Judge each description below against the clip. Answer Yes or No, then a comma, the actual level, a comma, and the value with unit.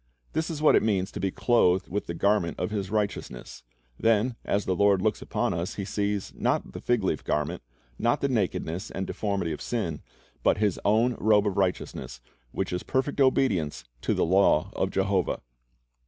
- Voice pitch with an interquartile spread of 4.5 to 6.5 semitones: No, average, 3.3 semitones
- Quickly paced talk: No, average, 185 wpm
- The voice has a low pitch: Yes, low, 100 Hz